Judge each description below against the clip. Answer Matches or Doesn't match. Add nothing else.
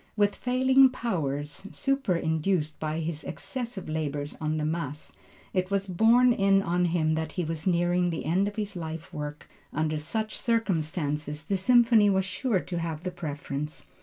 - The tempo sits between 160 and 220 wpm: Matches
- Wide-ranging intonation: Doesn't match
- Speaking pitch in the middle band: Matches